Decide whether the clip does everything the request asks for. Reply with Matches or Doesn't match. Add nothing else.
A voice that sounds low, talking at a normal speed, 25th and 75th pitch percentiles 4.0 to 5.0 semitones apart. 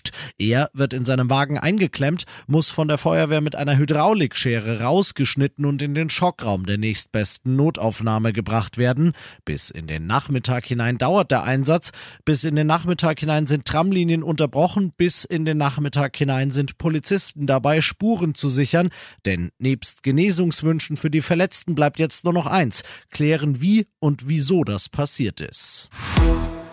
Doesn't match